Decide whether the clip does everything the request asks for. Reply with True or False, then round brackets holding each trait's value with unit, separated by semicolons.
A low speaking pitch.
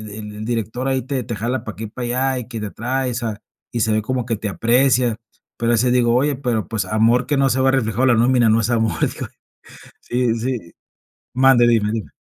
True (120 Hz)